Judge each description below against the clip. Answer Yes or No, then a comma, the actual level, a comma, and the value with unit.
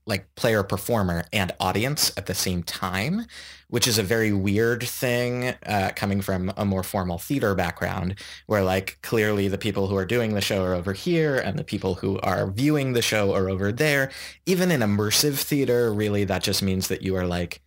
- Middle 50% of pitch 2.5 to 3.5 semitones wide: No, average, 4.3 semitones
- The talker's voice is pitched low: Yes, low, 100 Hz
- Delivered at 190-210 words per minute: Yes, average, 200 wpm